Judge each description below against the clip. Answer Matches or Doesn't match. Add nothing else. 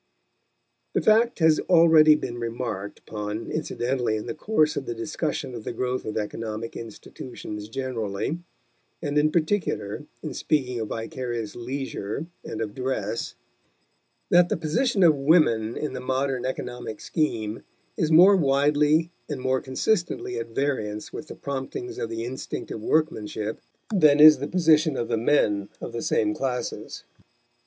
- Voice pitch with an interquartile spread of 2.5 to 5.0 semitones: Doesn't match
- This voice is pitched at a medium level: Doesn't match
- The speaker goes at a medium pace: Matches